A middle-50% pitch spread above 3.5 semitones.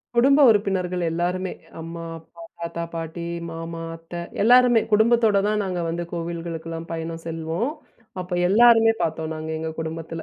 Yes: average, 4.0 semitones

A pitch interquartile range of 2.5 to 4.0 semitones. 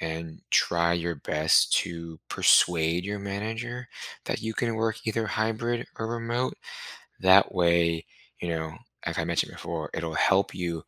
No: average, 5.1 semitones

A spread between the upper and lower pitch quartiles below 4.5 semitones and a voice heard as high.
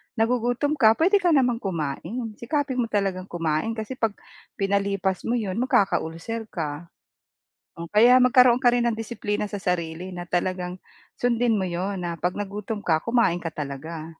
No: average, 5.2 semitones; high, 205 Hz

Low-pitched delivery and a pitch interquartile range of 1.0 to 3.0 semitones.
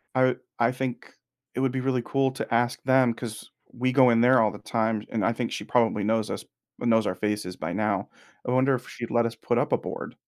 Yes: low, 120 Hz; narrow, 2.6 semitones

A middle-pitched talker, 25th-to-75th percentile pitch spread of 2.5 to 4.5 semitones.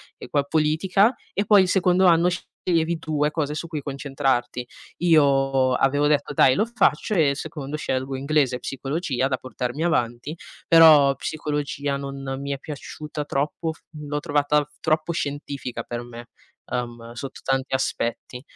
Yes: medium, 145 Hz; average, 2.8 semitones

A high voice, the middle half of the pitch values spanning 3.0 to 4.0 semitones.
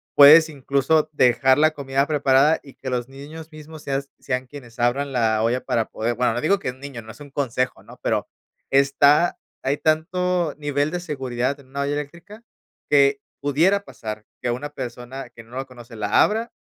No: medium, 140 Hz; average, 3.3 semitones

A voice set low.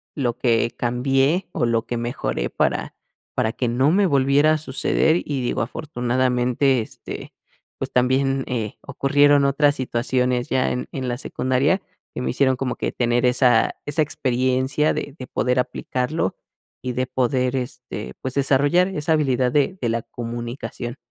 Yes: low, 130 Hz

